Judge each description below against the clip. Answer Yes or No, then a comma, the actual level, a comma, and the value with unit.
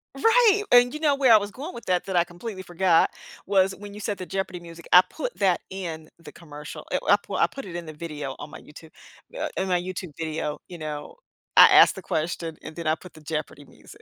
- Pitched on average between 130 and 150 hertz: No, medium, 180 Hz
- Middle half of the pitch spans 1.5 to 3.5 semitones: No, average, 4.2 semitones